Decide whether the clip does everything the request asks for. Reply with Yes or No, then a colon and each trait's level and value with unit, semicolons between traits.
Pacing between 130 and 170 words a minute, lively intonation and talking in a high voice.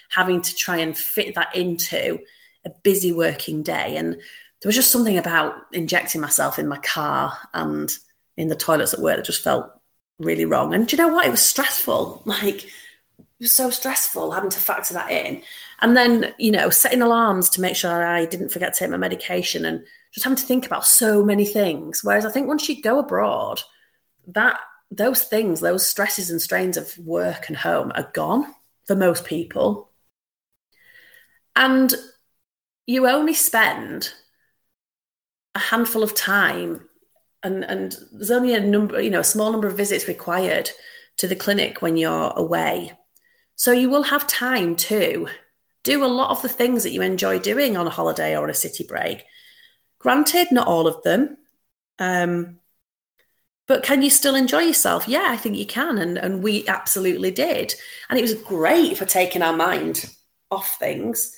No: average, 180 wpm; wide, 7.7 semitones; high, 215 Hz